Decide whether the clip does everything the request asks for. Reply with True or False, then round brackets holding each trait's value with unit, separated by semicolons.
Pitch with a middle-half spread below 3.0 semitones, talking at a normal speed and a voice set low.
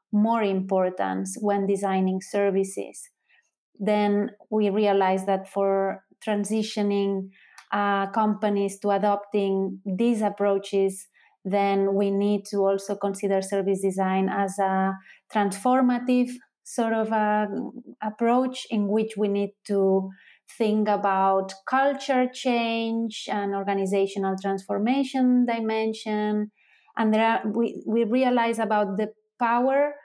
False (2.5 semitones; 110 wpm; 205 Hz)